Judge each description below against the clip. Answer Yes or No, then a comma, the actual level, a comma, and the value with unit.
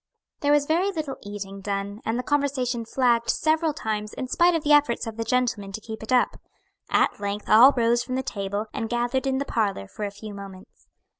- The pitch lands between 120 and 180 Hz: No, high, 235 Hz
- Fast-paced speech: Yes, fast, 215 wpm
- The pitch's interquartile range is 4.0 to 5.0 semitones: Yes, average, 4.6 semitones